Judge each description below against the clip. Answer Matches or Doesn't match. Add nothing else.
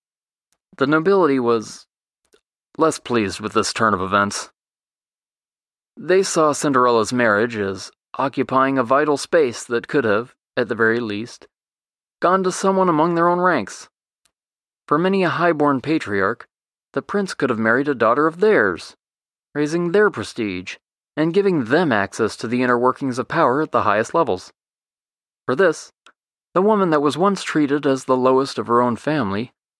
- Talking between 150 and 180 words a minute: Matches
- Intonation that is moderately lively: Doesn't match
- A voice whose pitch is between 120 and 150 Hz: Matches